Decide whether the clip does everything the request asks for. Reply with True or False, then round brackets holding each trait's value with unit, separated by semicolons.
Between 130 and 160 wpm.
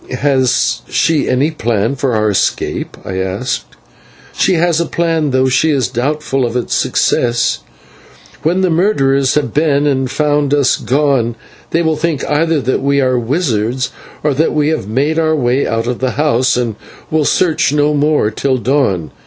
False (170 wpm)